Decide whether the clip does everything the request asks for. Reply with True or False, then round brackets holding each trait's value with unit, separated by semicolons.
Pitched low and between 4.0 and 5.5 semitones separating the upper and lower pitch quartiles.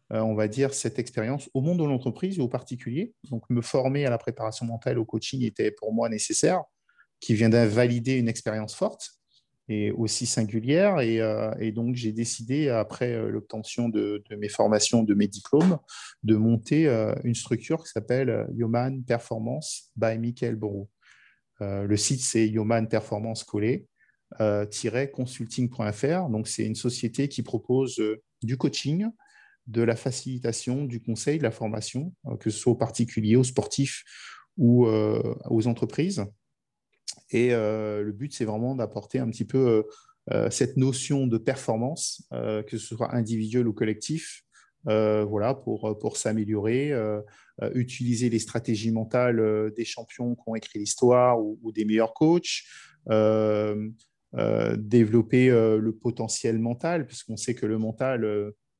False (115 Hz; 2.8 semitones)